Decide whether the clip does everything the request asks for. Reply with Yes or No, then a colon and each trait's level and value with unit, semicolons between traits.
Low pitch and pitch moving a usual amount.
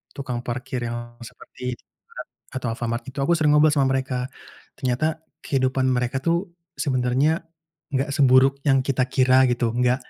No: low, 130 Hz; narrow, 1.9 semitones